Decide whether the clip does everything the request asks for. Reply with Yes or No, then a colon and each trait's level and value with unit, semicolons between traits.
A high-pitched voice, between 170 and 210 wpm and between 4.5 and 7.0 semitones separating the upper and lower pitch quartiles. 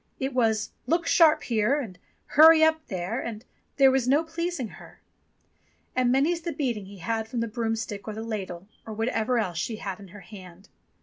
Yes: high, 230 Hz; average, 190 wpm; average, 5.2 semitones